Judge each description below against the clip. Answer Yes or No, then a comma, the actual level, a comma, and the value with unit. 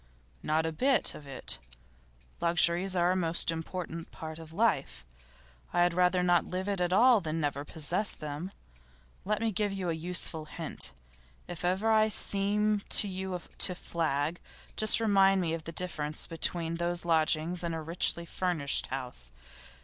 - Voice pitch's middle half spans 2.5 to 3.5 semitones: Yes, average, 2.9 semitones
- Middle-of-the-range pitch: Yes, medium, 175 Hz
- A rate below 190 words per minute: Yes, average, 160 wpm